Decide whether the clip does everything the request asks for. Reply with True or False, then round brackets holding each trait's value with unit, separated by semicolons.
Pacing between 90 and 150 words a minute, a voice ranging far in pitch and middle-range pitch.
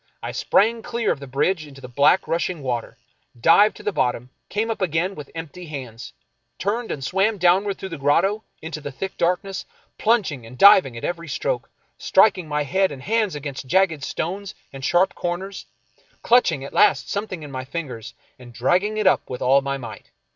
False (190 wpm; 6.2 semitones; 170 Hz)